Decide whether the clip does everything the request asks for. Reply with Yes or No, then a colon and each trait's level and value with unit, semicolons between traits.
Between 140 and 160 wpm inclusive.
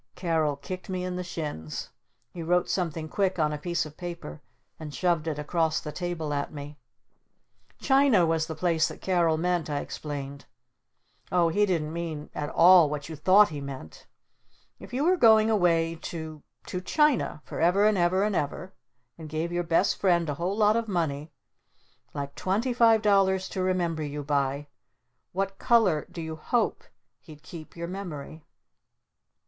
No: average, 170 wpm